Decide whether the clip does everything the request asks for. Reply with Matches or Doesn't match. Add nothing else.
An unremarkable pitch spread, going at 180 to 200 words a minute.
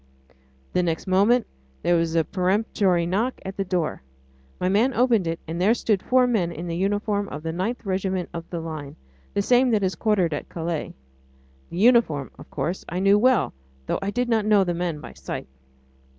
Matches